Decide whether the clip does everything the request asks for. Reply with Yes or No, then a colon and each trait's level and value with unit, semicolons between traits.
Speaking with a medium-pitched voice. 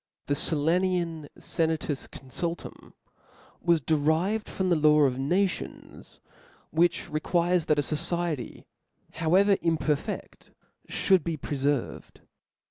Yes: medium, 160 Hz